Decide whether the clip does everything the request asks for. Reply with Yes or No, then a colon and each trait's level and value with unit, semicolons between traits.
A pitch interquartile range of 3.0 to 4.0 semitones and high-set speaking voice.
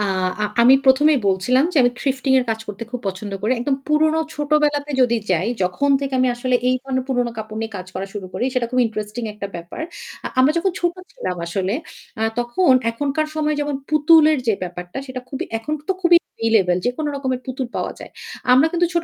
No: average, 5.3 semitones; very high, 255 Hz